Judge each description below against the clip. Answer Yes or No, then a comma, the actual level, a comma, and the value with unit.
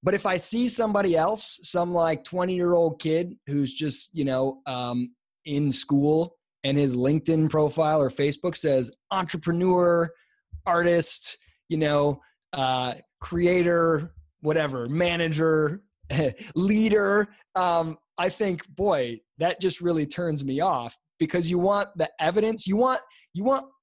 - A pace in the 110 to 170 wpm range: Yes, slow, 135 wpm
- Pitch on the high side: No, medium, 165 Hz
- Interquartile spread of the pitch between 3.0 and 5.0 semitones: Yes, average, 3.8 semitones